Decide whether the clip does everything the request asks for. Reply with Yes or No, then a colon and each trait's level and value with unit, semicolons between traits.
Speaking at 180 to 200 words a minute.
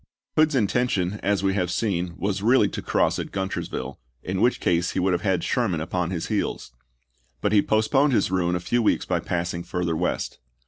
Yes: average, 195 wpm